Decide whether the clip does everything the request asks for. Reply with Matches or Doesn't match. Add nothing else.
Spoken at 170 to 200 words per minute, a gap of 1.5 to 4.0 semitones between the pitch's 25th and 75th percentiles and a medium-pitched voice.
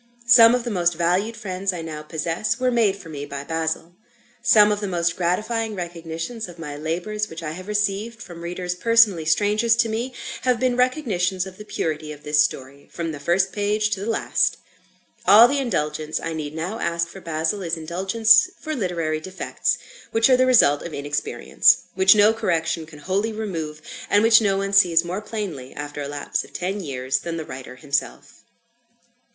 Doesn't match